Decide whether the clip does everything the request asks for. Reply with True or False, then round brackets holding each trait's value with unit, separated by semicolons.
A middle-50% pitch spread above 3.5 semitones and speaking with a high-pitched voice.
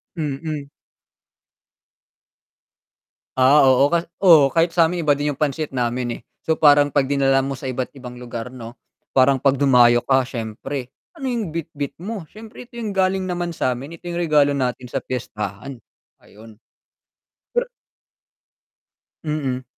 False (4.5 semitones; 140 Hz)